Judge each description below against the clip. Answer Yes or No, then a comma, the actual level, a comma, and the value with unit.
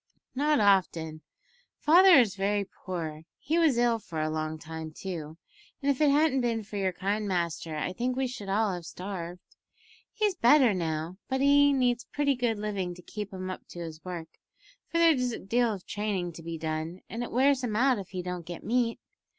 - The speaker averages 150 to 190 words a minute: No, average, 200 wpm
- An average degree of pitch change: No, wide, 6.5 semitones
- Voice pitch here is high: Yes, high, 205 Hz